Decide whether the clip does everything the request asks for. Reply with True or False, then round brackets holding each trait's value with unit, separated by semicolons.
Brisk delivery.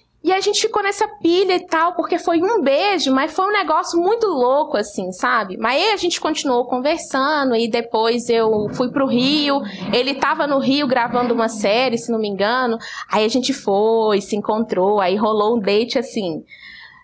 True (190 wpm)